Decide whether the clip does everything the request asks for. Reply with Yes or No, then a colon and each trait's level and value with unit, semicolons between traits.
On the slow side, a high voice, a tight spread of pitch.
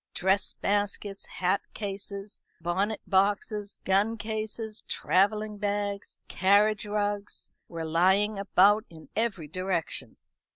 Yes: slow, 100 wpm; high, 200 Hz; narrow, 1.6 semitones